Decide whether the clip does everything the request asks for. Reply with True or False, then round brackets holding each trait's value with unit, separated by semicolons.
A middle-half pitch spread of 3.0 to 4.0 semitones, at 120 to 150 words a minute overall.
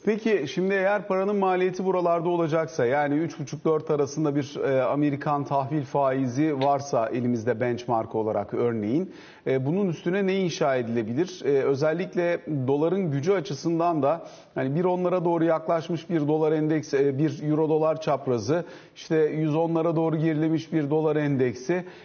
True (3.5 semitones; 130 wpm)